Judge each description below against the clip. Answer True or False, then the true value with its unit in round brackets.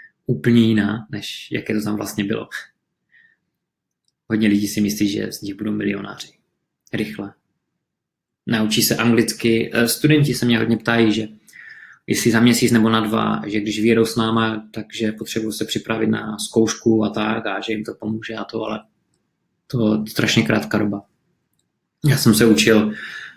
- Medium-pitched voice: False (110 Hz)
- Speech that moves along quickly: False (160 wpm)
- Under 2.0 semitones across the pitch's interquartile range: True (1.4 semitones)